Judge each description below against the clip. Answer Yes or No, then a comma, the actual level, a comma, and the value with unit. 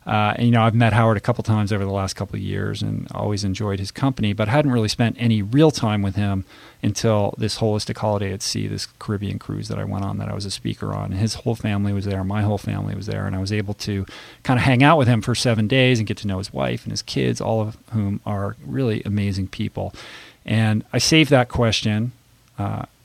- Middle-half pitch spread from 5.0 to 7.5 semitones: No, average, 2.8 semitones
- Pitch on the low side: Yes, low, 105 Hz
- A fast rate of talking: Yes, fast, 250 wpm